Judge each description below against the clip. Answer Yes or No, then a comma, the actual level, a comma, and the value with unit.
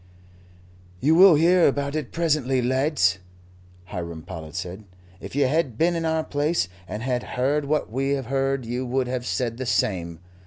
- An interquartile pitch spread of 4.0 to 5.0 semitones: Yes, average, 4.7 semitones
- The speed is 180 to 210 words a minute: No, average, 170 wpm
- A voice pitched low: Yes, low, 130 Hz